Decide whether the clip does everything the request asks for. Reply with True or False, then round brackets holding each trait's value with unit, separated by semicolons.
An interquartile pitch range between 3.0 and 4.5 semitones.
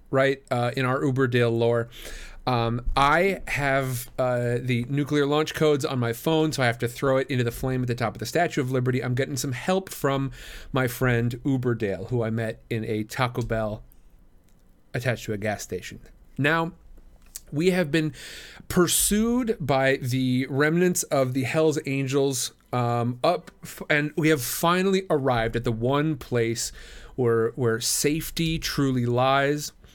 True (3.8 semitones)